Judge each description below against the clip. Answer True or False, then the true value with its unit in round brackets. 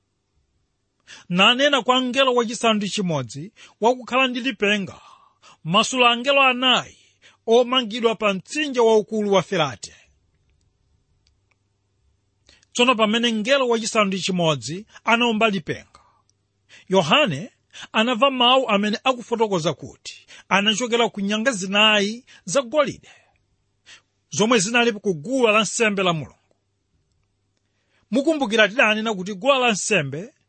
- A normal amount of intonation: False (8.8 semitones)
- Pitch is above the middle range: True (210 Hz)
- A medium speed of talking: False (85 wpm)